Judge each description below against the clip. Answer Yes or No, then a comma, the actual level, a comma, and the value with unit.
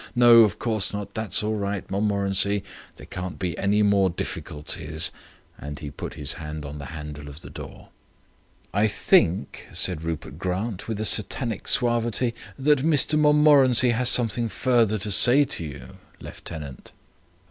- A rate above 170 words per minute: No, average, 155 wpm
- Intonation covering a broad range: Yes, wide, 6.3 semitones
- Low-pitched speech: Yes, low, 100 Hz